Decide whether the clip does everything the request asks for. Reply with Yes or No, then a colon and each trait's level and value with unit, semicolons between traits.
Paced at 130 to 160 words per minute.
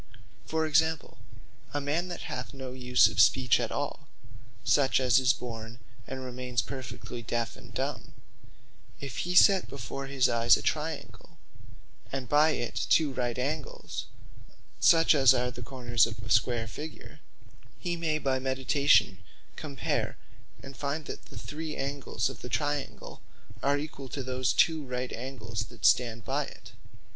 Yes: average, 155 wpm